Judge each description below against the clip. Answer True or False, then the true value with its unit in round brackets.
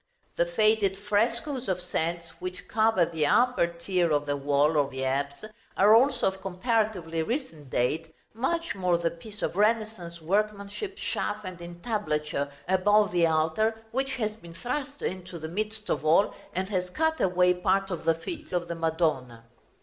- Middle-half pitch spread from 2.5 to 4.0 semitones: False (4.7 semitones)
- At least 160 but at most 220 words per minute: True (165 wpm)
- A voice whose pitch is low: False (185 Hz)